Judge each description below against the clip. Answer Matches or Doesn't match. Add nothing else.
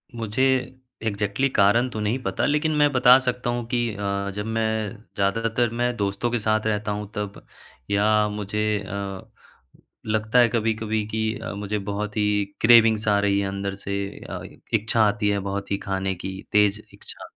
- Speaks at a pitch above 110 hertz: Doesn't match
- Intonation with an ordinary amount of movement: Doesn't match